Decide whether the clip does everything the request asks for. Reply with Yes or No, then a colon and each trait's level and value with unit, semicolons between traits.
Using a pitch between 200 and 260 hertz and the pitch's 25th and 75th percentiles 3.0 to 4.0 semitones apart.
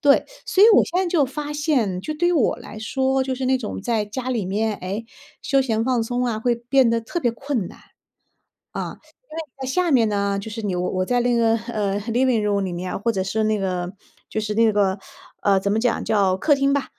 No: high, 230 Hz; average, 4.5 semitones